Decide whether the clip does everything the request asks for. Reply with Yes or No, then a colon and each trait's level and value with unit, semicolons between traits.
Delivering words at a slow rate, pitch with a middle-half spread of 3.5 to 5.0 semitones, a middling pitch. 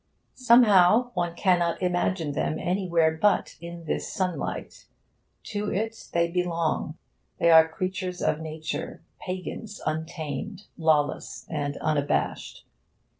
No: slow, 110 wpm; average, 2.9 semitones; medium, 170 Hz